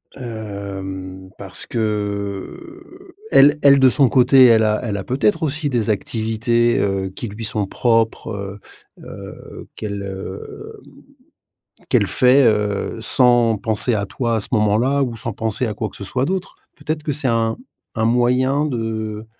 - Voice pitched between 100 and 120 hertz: Yes, low, 115 Hz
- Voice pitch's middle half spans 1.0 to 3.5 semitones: No, average, 3.9 semitones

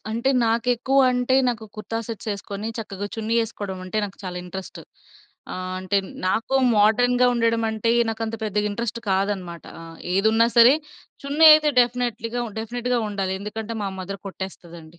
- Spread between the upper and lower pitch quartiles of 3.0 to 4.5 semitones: Yes, average, 3.3 semitones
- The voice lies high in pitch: Yes, high, 220 Hz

